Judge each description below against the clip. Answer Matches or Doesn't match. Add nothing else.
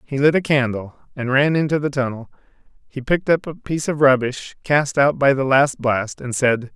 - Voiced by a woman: Doesn't match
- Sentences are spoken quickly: Matches